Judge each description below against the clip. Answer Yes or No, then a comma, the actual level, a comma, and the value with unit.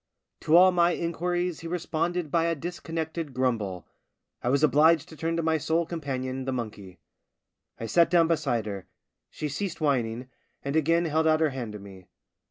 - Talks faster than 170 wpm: Yes, average, 180 wpm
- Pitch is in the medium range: Yes, medium, 155 Hz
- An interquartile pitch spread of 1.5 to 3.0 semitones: No, average, 4.6 semitones